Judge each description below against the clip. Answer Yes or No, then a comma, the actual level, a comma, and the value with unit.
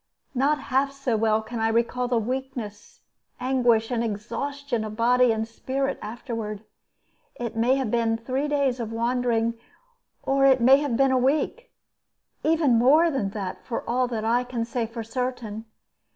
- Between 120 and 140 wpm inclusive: No, average, 165 wpm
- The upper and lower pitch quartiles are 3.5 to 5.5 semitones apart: No, average, 2.9 semitones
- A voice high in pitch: Yes, high, 245 Hz